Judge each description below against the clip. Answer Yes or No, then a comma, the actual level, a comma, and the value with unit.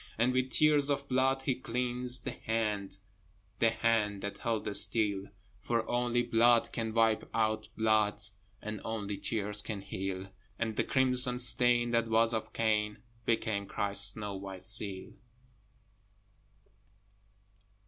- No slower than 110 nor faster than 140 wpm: Yes, slow, 135 wpm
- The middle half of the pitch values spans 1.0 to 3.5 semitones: Yes, average, 2.7 semitones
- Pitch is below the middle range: Yes, low, 110 Hz